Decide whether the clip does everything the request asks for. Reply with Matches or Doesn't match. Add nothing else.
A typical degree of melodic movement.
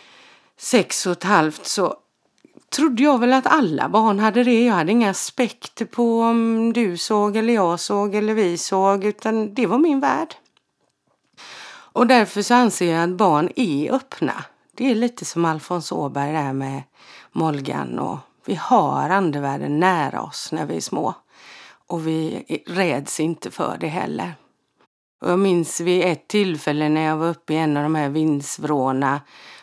Doesn't match